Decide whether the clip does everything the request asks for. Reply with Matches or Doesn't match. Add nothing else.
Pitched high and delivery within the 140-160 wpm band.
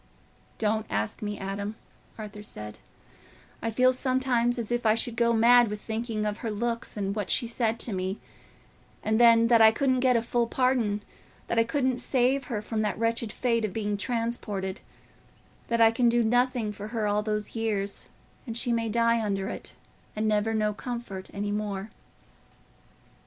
Doesn't match